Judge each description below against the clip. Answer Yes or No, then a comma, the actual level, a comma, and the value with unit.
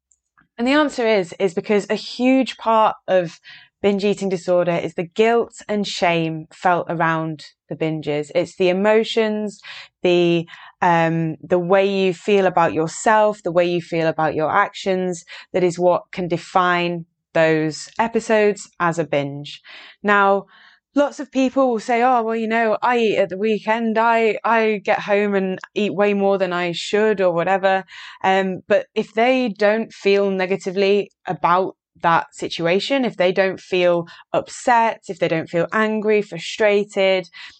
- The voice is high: Yes, high, 195 Hz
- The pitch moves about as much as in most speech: Yes, average, 3.8 semitones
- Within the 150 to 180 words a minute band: Yes, average, 160 wpm